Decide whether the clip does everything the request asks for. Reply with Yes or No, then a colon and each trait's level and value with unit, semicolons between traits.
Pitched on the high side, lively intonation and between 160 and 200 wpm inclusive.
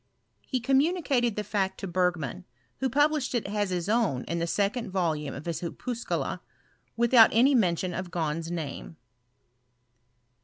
No: high, 195 Hz; wide, 6.1 semitones; average, 145 wpm